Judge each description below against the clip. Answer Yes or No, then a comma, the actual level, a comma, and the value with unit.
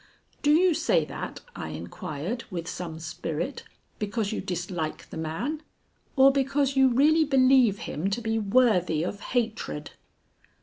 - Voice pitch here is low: No, high, 225 Hz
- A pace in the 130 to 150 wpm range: Yes, average, 140 wpm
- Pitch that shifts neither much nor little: No, wide, 7.4 semitones